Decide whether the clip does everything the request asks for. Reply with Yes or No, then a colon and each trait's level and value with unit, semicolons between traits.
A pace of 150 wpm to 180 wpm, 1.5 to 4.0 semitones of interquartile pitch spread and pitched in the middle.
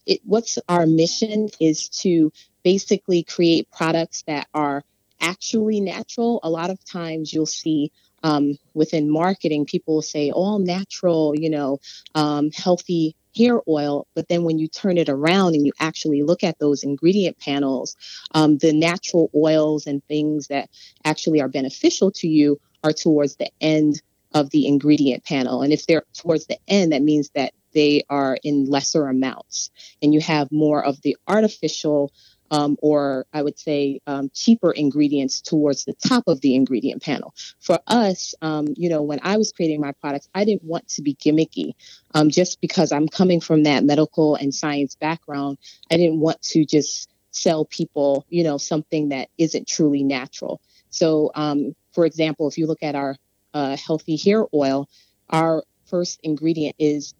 Yes: average, 170 wpm; average, 2.7 semitones; medium, 155 Hz